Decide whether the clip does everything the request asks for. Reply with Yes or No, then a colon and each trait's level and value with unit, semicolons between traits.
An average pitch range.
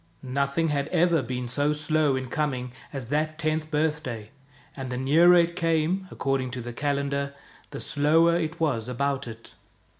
Yes: average, 3.4 semitones